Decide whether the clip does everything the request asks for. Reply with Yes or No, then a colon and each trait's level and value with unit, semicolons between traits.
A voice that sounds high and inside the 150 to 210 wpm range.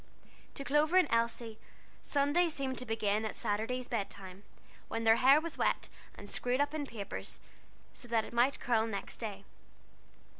Yes: high, 235 Hz; average, 160 wpm